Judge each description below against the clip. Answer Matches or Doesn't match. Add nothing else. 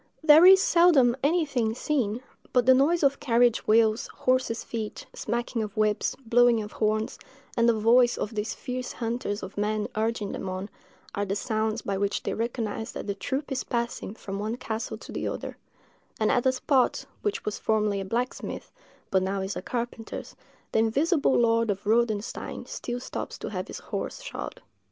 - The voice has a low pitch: Doesn't match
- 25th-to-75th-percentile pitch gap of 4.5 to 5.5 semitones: Doesn't match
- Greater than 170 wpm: Matches